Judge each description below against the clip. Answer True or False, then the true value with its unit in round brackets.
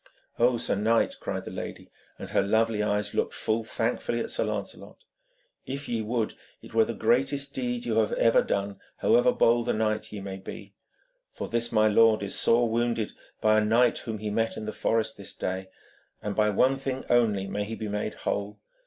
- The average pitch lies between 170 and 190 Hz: False (110 Hz)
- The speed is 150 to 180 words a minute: False (200 wpm)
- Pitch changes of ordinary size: False (2.0 semitones)